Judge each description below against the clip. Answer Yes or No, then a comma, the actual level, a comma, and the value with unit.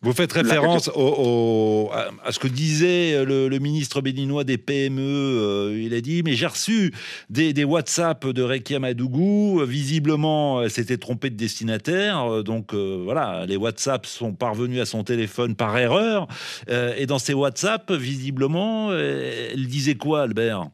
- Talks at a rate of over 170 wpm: No, average, 165 wpm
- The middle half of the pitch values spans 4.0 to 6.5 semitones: Yes, average, 4.4 semitones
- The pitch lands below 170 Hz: Yes, low, 135 Hz